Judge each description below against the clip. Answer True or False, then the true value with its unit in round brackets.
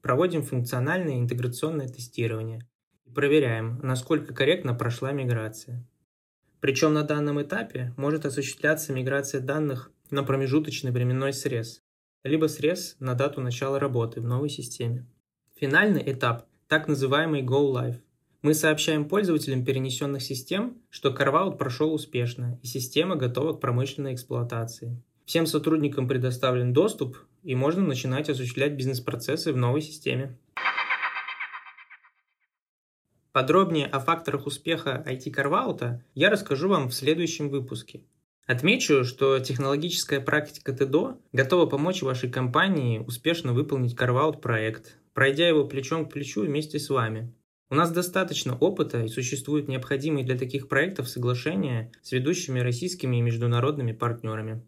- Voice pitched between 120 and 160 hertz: True (135 Hz)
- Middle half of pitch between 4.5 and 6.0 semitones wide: False (3.4 semitones)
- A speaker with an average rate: True (125 wpm)